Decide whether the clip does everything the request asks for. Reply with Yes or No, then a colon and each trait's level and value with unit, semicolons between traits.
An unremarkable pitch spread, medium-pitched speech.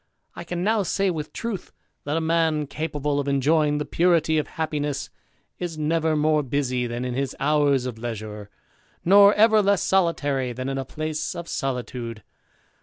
Yes: average, 3.7 semitones; medium, 150 Hz